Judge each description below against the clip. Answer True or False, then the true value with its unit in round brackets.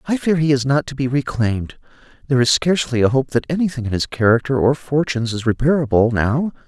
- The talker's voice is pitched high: False (135 Hz)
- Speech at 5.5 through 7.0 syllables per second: True (6.3 syllables/s)